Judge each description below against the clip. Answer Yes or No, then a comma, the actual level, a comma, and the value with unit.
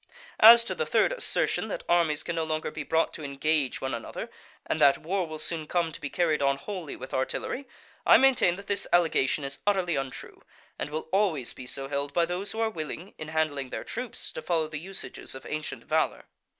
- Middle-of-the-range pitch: Yes, medium, 160 Hz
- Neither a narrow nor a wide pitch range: Yes, average, 4.5 semitones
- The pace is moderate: No, fast, 215 wpm